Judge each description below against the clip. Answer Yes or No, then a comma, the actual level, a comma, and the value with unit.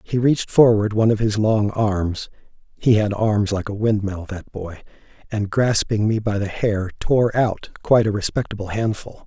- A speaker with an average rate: Yes, average, 170 wpm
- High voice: No, low, 105 Hz